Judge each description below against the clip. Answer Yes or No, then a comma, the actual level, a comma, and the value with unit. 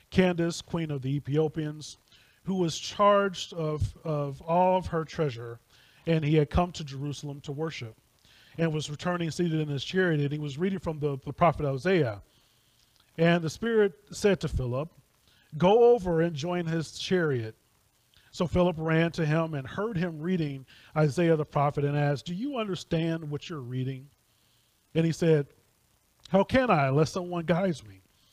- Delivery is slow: No, average, 170 wpm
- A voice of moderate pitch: Yes, medium, 155 Hz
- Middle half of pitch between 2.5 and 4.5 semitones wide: Yes, average, 4.1 semitones